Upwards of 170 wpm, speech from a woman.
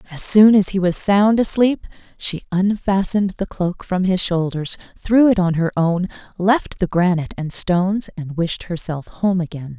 Yes: average, 180 wpm; female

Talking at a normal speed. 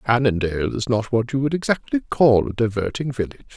Yes: average, 185 wpm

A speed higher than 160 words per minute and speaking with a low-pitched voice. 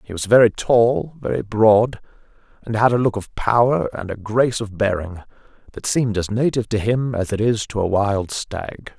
Yes: average, 200 wpm; low, 110 Hz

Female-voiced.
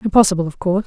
Yes: female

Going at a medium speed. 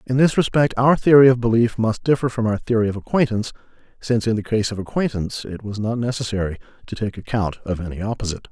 No: fast, 210 wpm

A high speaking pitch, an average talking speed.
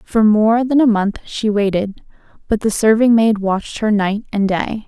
Yes: high, 215 Hz; average, 195 wpm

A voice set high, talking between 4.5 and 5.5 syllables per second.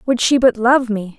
Yes: high, 235 Hz; 4.7 syllables/s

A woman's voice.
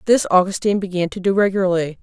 Yes: female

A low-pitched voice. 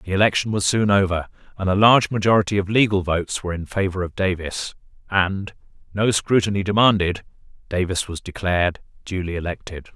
Yes: very low, 95 Hz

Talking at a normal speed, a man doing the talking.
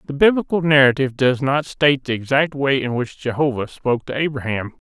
Yes: average, 185 wpm; male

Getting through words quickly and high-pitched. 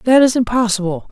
No: average, 160 wpm; high, 220 Hz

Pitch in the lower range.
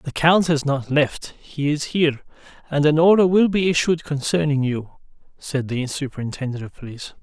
No: medium, 145 Hz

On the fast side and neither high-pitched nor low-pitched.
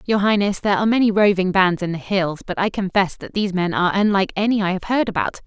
No: fast, 250 wpm; high, 195 Hz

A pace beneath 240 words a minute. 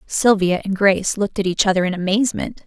Yes: average, 200 wpm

